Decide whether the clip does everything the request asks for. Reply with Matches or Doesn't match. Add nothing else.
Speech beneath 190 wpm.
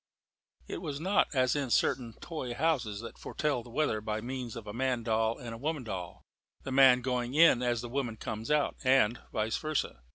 Doesn't match